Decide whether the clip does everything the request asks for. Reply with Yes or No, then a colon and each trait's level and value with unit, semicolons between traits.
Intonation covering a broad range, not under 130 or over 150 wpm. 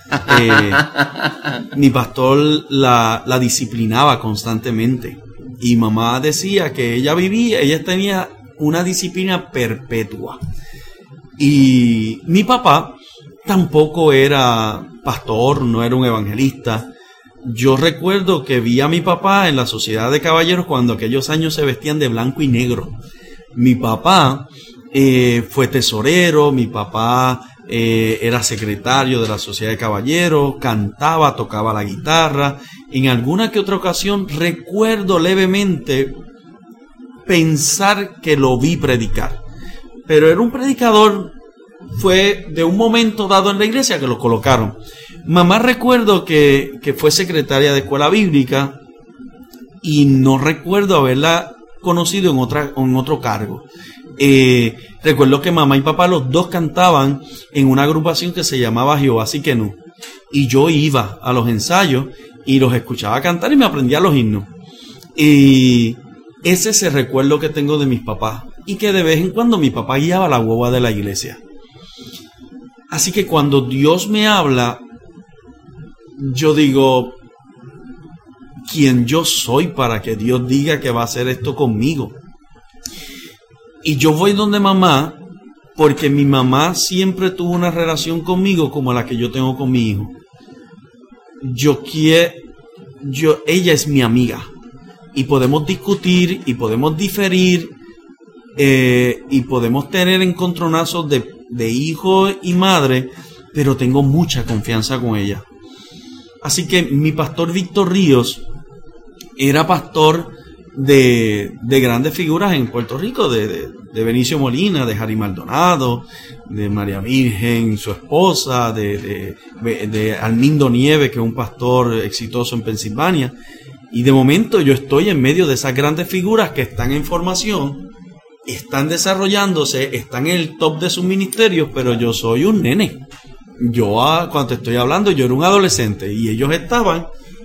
Yes: wide, 5.9 semitones; average, 140 wpm